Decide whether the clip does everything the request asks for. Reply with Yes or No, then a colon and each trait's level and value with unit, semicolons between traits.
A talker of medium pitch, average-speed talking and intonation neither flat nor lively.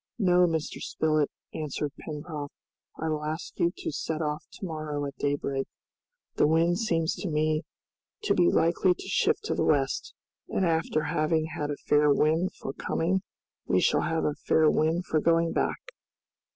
No: medium, 155 Hz; average, 170 wpm; narrow, 2.0 semitones